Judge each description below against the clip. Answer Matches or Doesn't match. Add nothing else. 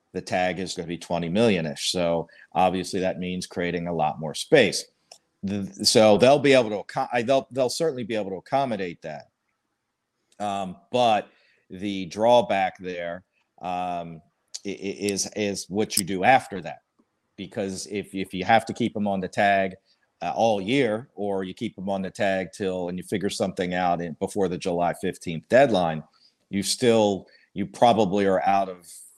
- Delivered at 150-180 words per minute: Matches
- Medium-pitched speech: Doesn't match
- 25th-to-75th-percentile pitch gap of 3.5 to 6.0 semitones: Doesn't match